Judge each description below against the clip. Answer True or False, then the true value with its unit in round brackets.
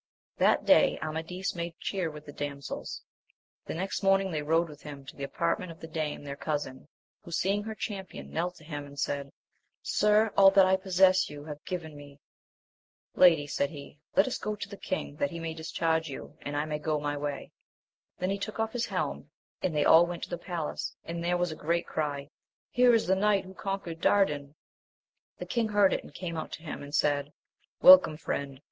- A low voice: False (165 Hz)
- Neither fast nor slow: False (210 wpm)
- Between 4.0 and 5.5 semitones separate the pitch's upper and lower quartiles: True (4.4 semitones)